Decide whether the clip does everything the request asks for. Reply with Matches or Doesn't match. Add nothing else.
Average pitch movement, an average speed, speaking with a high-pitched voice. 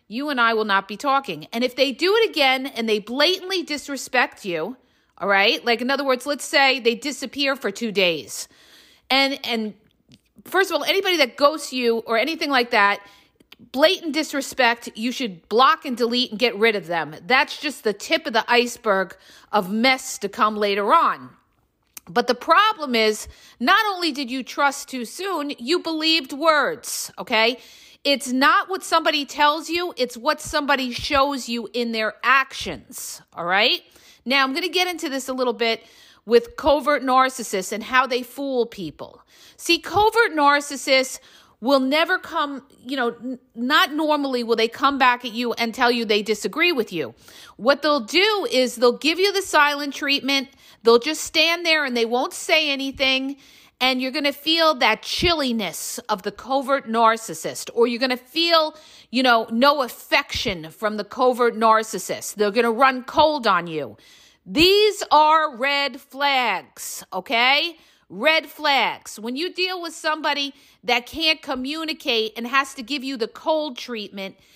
Matches